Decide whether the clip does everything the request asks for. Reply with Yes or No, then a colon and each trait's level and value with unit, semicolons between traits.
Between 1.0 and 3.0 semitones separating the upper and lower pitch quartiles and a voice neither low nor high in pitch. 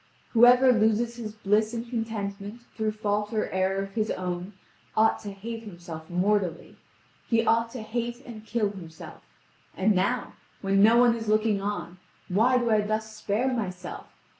No: average, 2.7 semitones; high, 215 Hz